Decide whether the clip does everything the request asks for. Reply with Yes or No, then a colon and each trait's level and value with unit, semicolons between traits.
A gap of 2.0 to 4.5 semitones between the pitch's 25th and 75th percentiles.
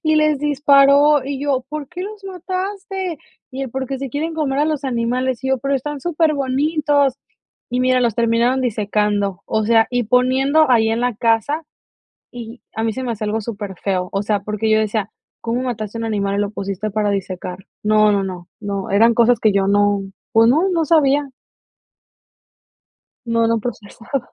No: average, 5.0 semitones